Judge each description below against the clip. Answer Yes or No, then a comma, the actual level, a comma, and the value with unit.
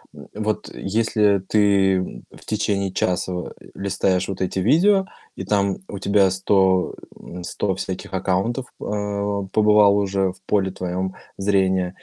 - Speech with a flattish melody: Yes, narrow, 1.6 semitones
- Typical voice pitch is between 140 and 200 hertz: No, low, 100 Hz